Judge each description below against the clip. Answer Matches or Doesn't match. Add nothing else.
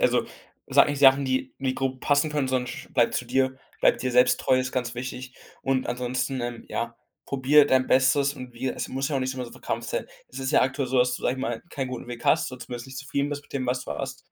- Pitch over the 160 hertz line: Doesn't match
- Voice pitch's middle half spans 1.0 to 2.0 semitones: Matches